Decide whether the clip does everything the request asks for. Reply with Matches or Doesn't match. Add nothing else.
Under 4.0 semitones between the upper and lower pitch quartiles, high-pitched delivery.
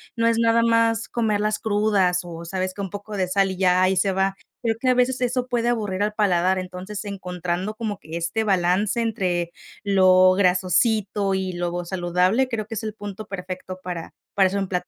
Matches